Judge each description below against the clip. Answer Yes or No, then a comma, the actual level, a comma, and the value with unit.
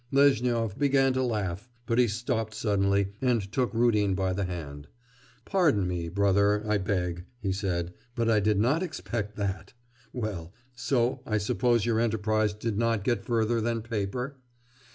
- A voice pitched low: Yes, low, 110 Hz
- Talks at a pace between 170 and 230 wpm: No, average, 155 wpm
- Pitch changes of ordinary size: Yes, average, 3.3 semitones